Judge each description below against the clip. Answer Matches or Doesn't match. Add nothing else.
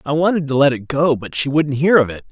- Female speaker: Doesn't match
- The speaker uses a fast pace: Matches